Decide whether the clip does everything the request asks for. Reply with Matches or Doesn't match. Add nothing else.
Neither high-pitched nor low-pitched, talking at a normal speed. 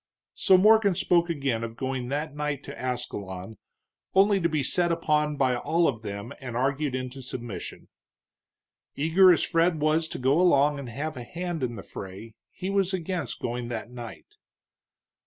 Matches